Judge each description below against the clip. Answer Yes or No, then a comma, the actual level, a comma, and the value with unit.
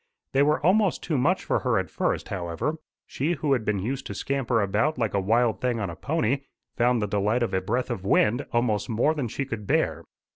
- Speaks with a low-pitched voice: Yes, low, 120 Hz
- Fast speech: Yes, fast, 225 wpm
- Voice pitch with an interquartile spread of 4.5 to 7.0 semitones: Yes, average, 4.9 semitones